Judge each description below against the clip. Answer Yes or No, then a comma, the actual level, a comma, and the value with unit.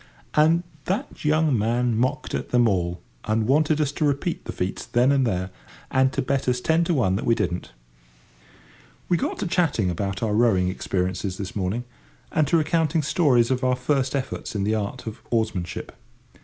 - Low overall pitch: Yes, low, 125 Hz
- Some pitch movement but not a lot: No, wide, 6.5 semitones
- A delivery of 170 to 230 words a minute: Yes, average, 185 wpm